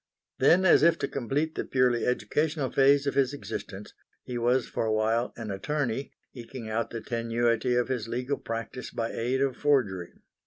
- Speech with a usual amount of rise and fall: Yes, average, 3.1 semitones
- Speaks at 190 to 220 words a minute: No, average, 180 wpm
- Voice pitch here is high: No, low, 125 Hz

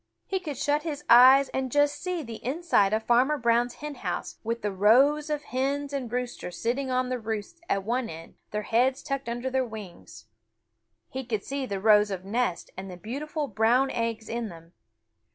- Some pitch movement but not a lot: Yes, average, 4.4 semitones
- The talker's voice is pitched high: Yes, high, 245 Hz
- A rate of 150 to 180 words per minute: No, average, 190 wpm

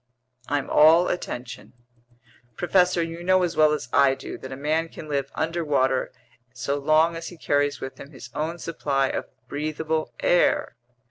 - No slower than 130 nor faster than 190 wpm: Yes, average, 160 wpm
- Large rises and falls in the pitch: No, average, 3.1 semitones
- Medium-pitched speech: Yes, medium, 155 Hz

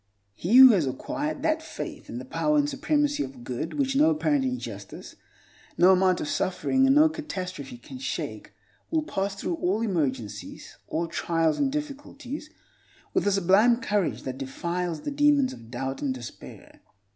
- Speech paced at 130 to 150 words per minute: No, average, 165 wpm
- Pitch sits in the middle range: No, high, 205 Hz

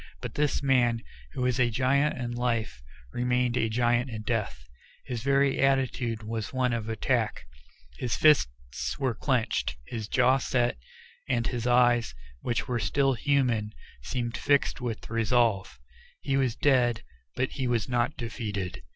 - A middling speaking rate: Yes, average, 150 wpm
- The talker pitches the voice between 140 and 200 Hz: No, low, 120 Hz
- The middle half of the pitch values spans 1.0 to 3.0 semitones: Yes, narrow, 2.4 semitones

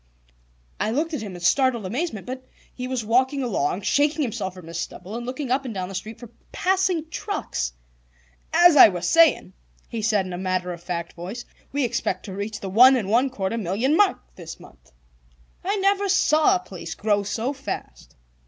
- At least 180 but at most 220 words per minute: Yes, average, 195 wpm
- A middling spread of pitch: No, wide, 7.2 semitones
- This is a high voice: Yes, high, 230 Hz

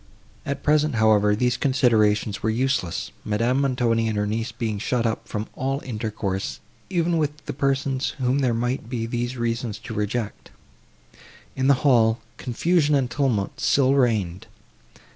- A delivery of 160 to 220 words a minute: No, average, 150 wpm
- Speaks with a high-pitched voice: No, low, 120 Hz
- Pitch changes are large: No, average, 3.7 semitones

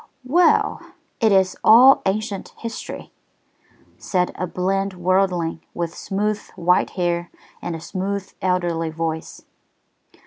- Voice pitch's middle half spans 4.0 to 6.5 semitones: No, narrow, 2.5 semitones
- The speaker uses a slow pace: Yes, slow, 110 wpm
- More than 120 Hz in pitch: Yes, medium, 185 Hz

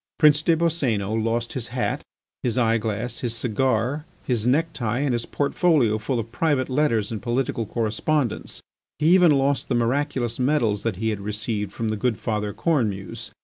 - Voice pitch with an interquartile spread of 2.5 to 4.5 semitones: Yes, average, 4.2 semitones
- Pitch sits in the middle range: No, low, 120 Hz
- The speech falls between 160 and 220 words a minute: Yes, average, 170 wpm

